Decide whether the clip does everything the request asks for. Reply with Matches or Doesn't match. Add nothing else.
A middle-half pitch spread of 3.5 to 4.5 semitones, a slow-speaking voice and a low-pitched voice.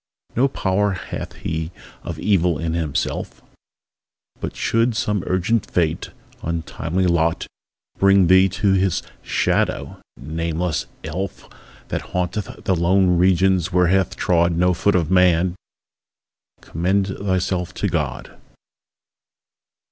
Doesn't match